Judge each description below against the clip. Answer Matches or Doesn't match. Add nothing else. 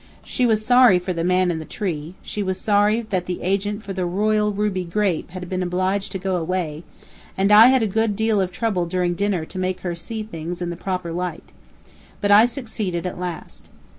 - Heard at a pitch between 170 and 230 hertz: Matches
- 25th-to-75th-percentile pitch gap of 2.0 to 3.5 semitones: Matches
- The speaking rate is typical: Doesn't match